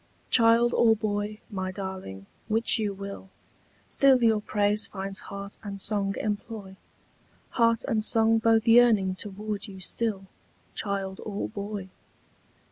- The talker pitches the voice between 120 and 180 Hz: No, high, 205 Hz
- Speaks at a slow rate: Yes, slow, 125 wpm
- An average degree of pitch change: No, narrow, 2.3 semitones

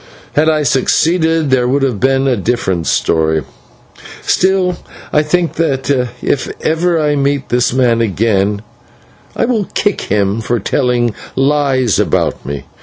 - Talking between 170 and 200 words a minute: No, average, 140 wpm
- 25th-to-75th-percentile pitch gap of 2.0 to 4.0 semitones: No, average, 5.2 semitones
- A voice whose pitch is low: Yes, low, 130 Hz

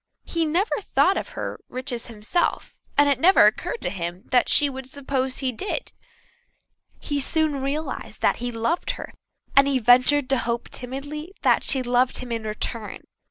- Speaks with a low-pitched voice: No, very high, 265 Hz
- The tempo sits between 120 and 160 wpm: No, average, 170 wpm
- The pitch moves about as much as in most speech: Yes, average, 3.3 semitones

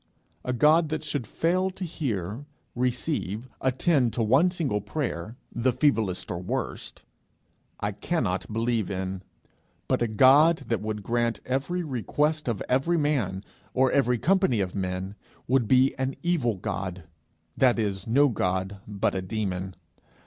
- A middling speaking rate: Yes, average, 145 wpm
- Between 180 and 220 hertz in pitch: No, low, 120 Hz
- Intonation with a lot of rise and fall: Yes, wide, 6.3 semitones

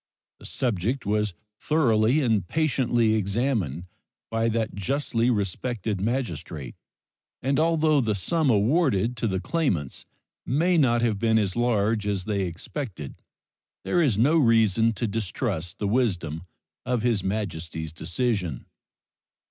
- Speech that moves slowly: Yes, slow, 125 wpm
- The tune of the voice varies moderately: Yes, average, 4.7 semitones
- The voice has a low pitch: Yes, low, 110 Hz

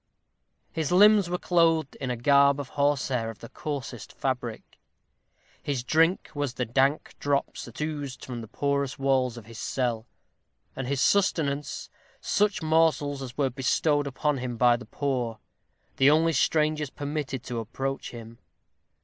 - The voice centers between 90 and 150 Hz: Yes, medium, 140 Hz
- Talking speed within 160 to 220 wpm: No, average, 150 wpm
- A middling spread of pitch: Yes, average, 3.3 semitones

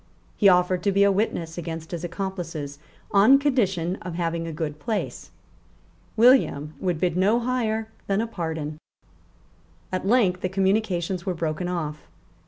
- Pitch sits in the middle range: Yes, medium, 180 Hz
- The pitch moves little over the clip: No, average, 3.6 semitones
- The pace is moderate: Yes, average, 150 wpm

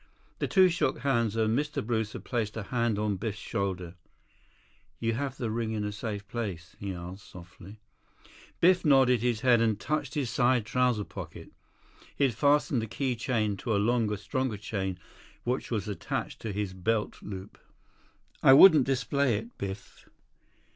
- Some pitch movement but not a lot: Yes, average, 3.8 semitones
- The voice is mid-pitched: No, low, 115 Hz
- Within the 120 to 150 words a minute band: No, average, 165 wpm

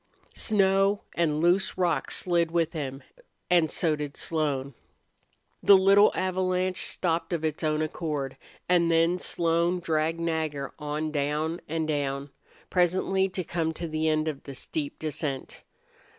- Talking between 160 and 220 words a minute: No, average, 140 wpm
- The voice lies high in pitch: No, medium, 165 Hz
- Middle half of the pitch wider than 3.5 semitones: No, average, 2.7 semitones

